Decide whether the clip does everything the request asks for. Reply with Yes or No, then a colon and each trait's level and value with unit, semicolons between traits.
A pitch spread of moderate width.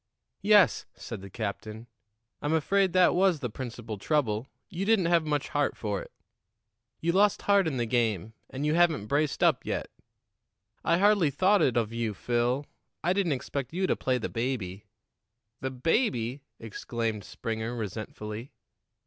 No: wide, 7.1 semitones